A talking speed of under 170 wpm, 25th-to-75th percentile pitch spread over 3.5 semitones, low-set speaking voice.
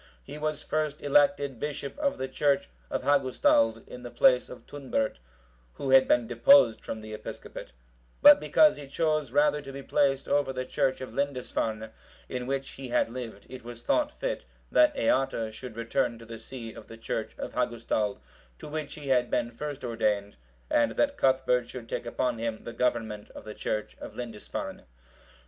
No: average, 180 wpm; average, 3.9 semitones; low, 130 Hz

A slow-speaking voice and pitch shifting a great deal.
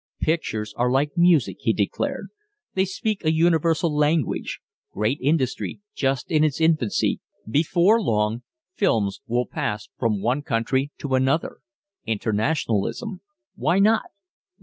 Yes: slow, 125 wpm; wide, 6.3 semitones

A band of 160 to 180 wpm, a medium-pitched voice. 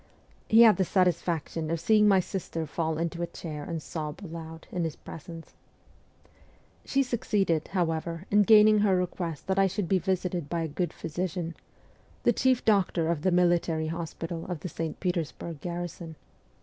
Yes: average, 165 wpm; medium, 170 Hz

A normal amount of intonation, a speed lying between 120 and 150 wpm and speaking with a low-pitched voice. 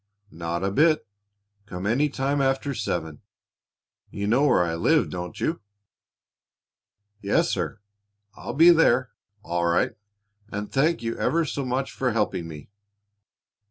No: wide, 8.0 semitones; slow, 135 wpm; low, 115 Hz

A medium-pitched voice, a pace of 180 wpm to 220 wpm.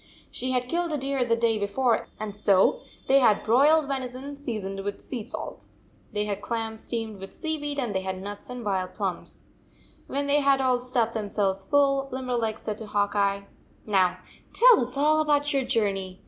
No: high, 235 Hz; average, 190 wpm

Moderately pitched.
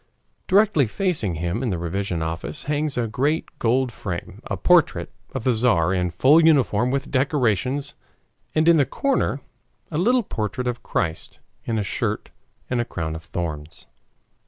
No: low, 120 Hz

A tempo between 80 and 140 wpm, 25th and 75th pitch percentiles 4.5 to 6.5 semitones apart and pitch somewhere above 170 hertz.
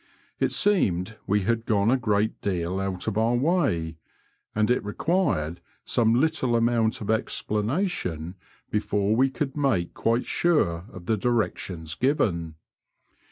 No: slow, 135 wpm; average, 5.2 semitones; low, 110 Hz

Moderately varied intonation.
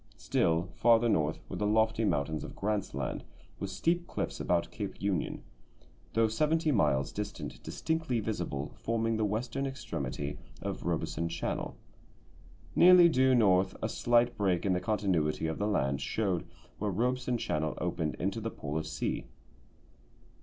No: wide, 6.0 semitones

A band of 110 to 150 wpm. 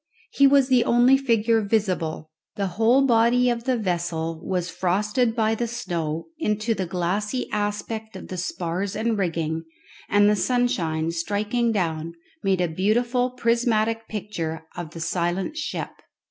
Yes: average, 145 wpm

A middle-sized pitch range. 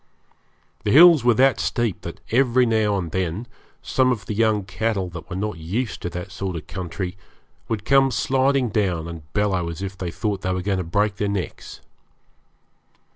Yes: average, 4.2 semitones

